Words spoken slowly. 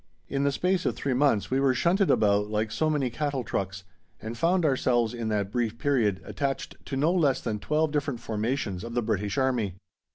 No: average, 200 wpm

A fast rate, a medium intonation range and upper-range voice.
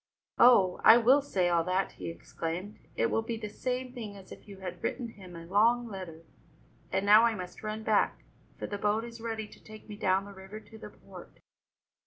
Yes: fast, 215 wpm; average, 3.3 semitones; high, 210 Hz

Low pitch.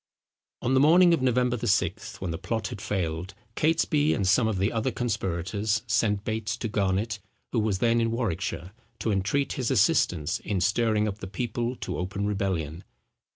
Yes: low, 110 Hz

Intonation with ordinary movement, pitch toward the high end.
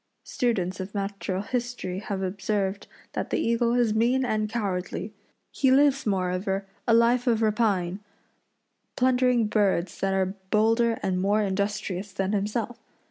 Yes: average, 3.5 semitones; high, 210 Hz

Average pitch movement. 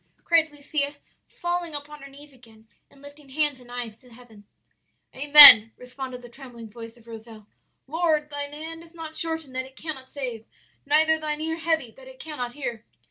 Yes: average, 4.0 semitones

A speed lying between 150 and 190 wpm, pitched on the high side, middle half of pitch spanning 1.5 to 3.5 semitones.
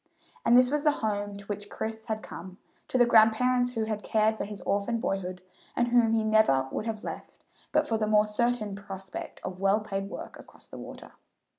No: fast, 205 wpm; high, 215 Hz; narrow, 2.5 semitones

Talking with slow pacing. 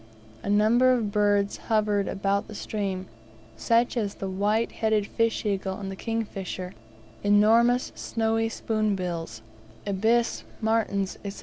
Yes: slow, 120 wpm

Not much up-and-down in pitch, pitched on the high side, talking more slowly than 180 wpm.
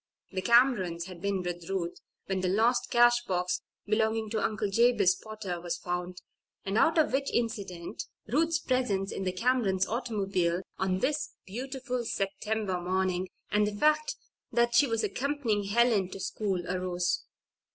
No: average, 4.5 semitones; high, 205 Hz; average, 150 wpm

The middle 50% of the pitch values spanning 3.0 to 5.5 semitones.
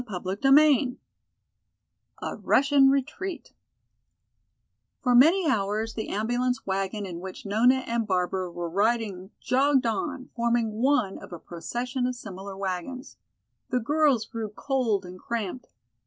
Yes: average, 5.0 semitones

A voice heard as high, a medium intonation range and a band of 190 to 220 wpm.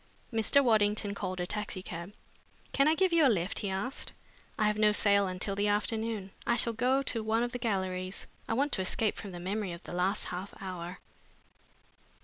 Yes: high, 205 Hz; average, 3.4 semitones; average, 195 wpm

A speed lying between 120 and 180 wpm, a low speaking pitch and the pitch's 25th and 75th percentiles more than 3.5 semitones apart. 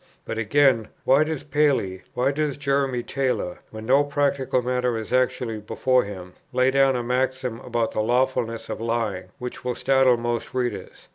No: average, 165 wpm; low, 125 Hz; average, 2.9 semitones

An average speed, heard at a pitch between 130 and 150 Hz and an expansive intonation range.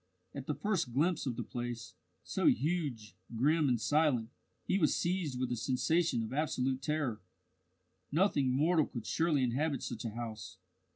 No: average, 160 wpm; low, 135 Hz; average, 4.8 semitones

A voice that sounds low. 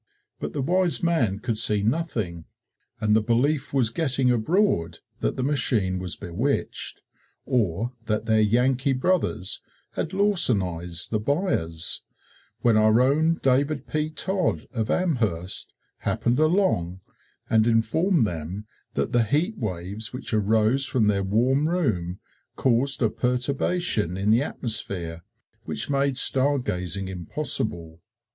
Yes: low, 115 Hz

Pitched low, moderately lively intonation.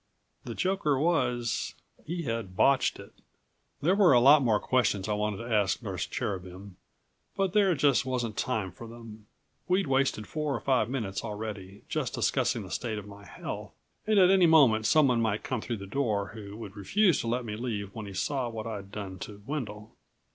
Yes: low, 115 Hz; average, 5.0 semitones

